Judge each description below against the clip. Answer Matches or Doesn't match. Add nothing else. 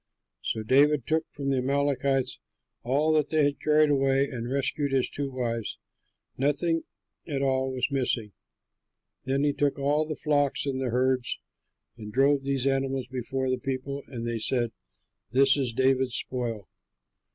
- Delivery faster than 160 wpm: Doesn't match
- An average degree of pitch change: Doesn't match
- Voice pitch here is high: Doesn't match